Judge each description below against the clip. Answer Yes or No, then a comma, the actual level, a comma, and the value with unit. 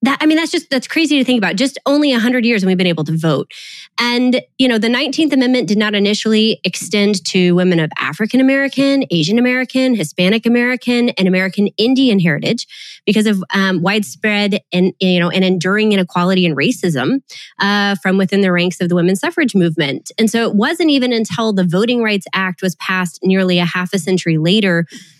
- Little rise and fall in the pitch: No, average, 5.0 semitones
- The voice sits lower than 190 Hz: No, high, 205 Hz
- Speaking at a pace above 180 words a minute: Yes, average, 200 wpm